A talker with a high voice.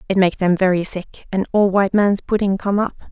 Yes: high, 195 Hz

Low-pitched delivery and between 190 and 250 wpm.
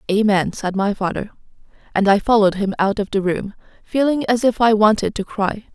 No: high, 210 Hz; average, 200 wpm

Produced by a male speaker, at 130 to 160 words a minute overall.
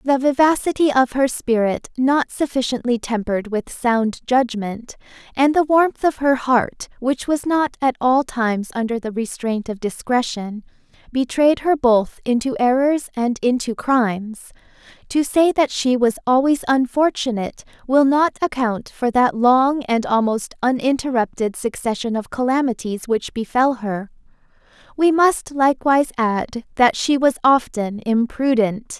No: female; average, 140 wpm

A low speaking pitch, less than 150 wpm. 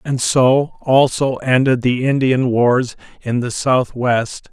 Yes: low, 125 Hz; slow, 135 wpm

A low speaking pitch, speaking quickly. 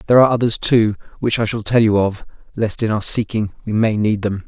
Yes: low, 110 Hz; fast, 240 wpm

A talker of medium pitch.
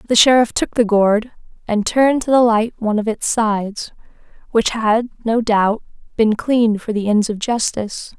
No: high, 225 Hz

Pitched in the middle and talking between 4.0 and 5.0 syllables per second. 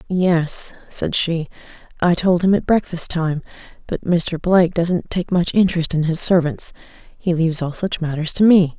Yes: medium, 170 Hz; 4.6 syllables/s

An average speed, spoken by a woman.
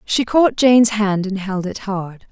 No: fast, 210 wpm; female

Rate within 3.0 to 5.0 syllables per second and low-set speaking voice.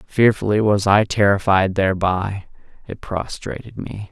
Yes: 4.4 syllables/s; low, 100 Hz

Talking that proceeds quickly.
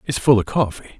Yes: fast, 240 wpm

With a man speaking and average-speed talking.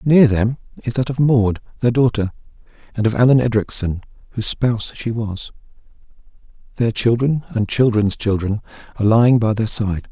Yes: male; average, 155 wpm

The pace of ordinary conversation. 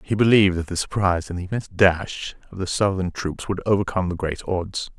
No: fast, 215 wpm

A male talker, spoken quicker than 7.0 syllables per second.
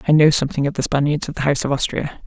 No: female; 7.7 syllables/s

